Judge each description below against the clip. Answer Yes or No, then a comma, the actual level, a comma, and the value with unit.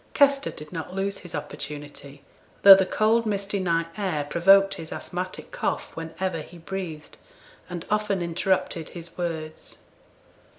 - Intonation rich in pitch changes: No, average, 3.5 semitones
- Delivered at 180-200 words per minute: No, average, 140 wpm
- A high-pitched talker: No, medium, 175 Hz